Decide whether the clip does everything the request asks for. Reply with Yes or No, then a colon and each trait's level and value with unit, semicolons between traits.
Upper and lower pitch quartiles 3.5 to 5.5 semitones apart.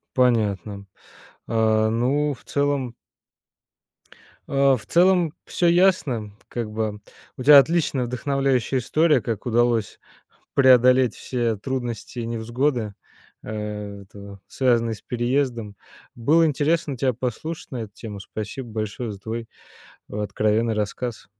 Yes: average, 4.0 semitones